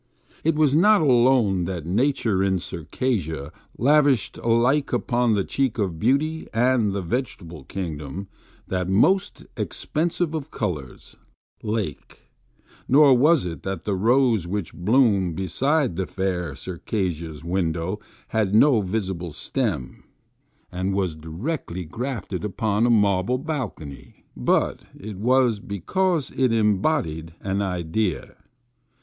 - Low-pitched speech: Yes, low, 105 Hz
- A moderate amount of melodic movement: No, wide, 6.4 semitones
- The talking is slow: Yes, slow, 120 wpm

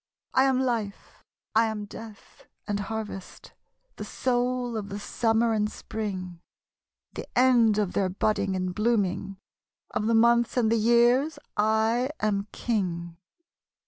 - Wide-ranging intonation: No, average, 2.8 semitones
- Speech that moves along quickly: No, slow, 135 wpm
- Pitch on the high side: Yes, high, 220 Hz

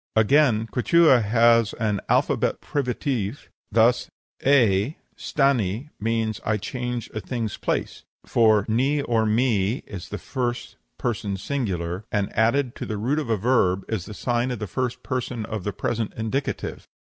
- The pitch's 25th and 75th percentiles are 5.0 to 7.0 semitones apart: No, average, 3.1 semitones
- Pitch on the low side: Yes, low, 115 Hz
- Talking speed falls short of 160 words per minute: Yes, average, 150 wpm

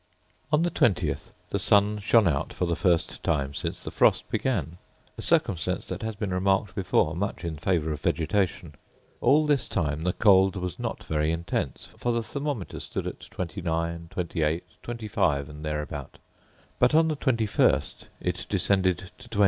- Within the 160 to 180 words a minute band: Yes, average, 165 wpm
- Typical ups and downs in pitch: Yes, average, 4.9 semitones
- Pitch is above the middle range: No, very low, 90 Hz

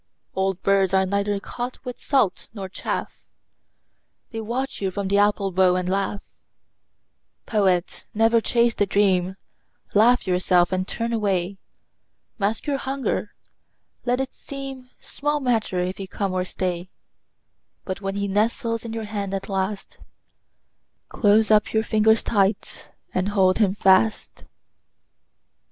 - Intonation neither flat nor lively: Yes, average, 3.0 semitones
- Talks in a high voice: Yes, high, 200 Hz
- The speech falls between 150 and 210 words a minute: No, average, 140 wpm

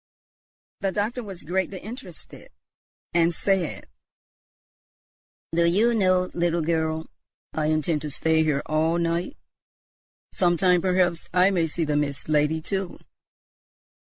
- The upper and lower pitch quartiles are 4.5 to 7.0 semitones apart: No, average, 2.9 semitones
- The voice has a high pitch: No, medium, 170 Hz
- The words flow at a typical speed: No, slow, 120 wpm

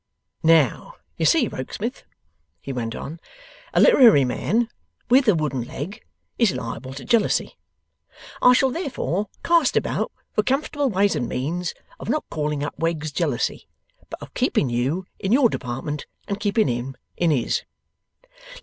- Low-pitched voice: No, medium, 165 Hz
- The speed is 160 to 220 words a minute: No, average, 150 wpm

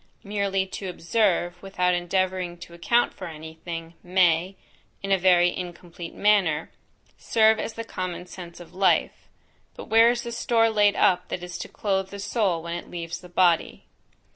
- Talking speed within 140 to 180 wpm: Yes, average, 170 wpm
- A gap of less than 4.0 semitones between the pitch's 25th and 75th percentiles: Yes, narrow, 2.5 semitones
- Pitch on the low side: No, medium, 185 Hz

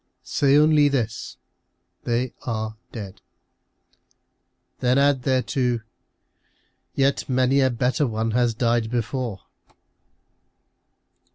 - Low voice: Yes, low, 125 Hz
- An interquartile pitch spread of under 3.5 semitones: Yes, average, 2.9 semitones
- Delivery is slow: Yes, slow, 100 wpm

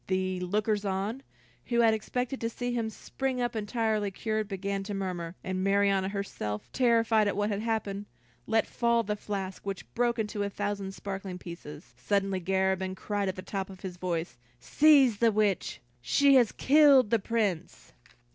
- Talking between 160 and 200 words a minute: Yes, average, 170 wpm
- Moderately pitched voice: No, high, 205 Hz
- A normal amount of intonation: Yes, average, 3.1 semitones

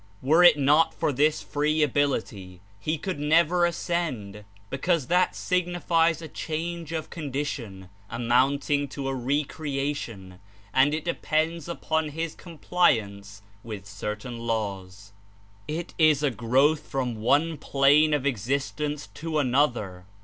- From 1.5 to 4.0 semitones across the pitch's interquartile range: No, average, 5.2 semitones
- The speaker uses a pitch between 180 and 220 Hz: No, medium, 145 Hz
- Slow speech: Yes, slow, 130 wpm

